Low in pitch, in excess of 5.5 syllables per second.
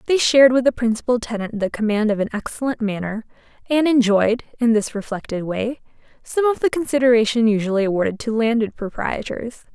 No: high, 230 Hz; 5.8 syllables/s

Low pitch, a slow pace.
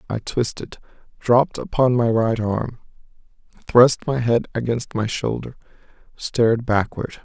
Yes: low, 115 Hz; slow, 125 wpm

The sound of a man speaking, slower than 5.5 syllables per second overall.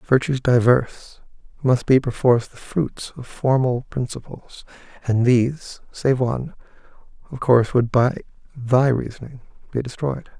Yes: male; 4.6 syllables/s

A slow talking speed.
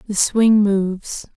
Yes: slow, 130 wpm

